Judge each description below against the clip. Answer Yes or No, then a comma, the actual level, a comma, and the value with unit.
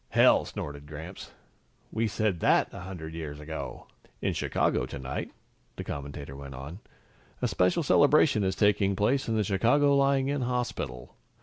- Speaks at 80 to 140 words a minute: No, average, 150 wpm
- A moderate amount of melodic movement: No, wide, 8.7 semitones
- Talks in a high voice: No, very low, 95 Hz